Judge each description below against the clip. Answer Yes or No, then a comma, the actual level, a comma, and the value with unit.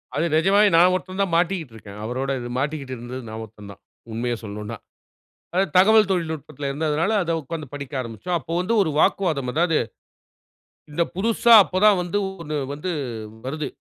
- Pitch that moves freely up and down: Yes, wide, 6.0 semitones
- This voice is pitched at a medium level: Yes, medium, 155 Hz